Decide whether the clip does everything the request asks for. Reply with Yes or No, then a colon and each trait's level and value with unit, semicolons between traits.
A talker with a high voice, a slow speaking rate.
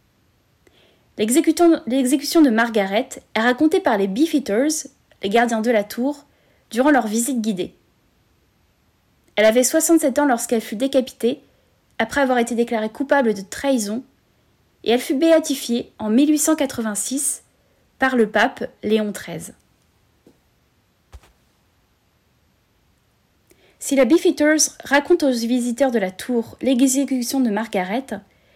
Yes: very high, 250 Hz; slow, 115 wpm